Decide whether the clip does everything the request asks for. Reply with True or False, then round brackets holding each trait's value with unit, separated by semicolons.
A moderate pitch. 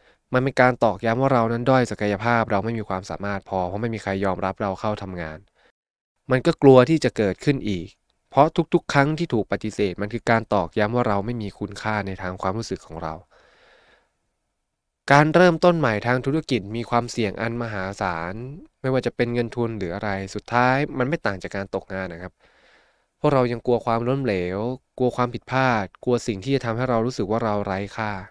False (115 Hz)